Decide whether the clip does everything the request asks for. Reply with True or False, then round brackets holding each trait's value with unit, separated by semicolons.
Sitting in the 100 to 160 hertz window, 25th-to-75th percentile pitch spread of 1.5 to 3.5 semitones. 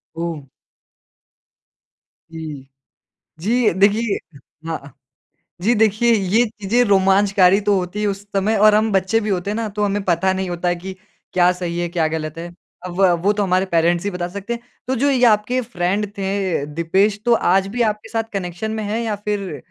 False (195 Hz; 3.2 semitones)